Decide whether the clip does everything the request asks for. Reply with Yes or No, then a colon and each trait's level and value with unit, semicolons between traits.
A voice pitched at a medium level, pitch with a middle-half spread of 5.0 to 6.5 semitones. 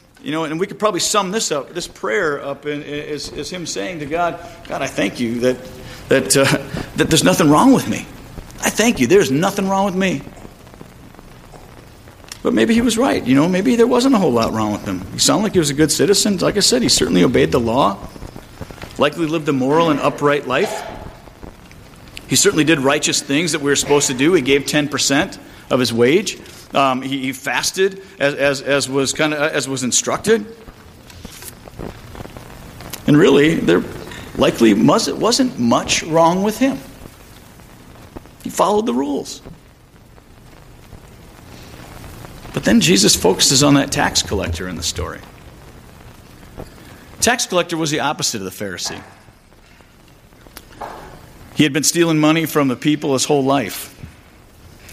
Yes: medium, 150 Hz; average, 5.3 semitones